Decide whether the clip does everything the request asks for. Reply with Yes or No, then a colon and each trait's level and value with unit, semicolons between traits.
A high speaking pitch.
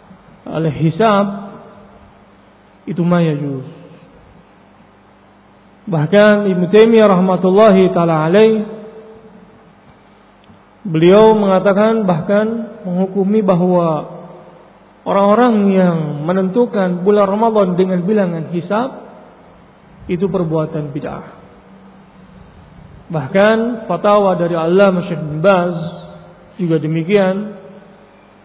Yes: high, 195 Hz